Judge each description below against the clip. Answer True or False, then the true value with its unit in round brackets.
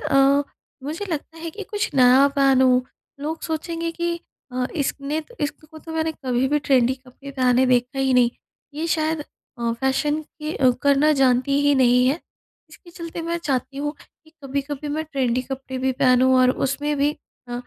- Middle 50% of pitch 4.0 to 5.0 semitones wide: False (3.3 semitones)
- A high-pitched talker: True (280 Hz)